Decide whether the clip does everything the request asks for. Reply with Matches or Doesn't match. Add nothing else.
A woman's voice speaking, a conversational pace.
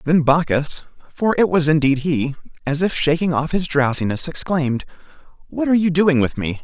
Doesn't match